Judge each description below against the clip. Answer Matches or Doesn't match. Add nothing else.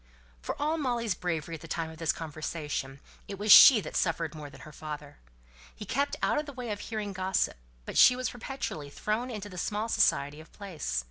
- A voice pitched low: Doesn't match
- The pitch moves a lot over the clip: Matches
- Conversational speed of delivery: Doesn't match